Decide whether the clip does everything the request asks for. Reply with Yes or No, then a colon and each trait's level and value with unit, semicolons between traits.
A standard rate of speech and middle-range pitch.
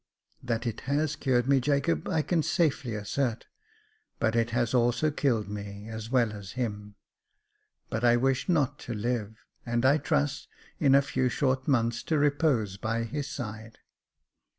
No: average, 170 wpm; low, 120 Hz